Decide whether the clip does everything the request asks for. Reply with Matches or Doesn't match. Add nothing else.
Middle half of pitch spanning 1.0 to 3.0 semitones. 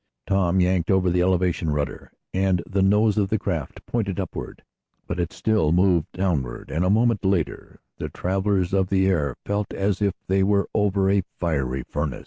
Matches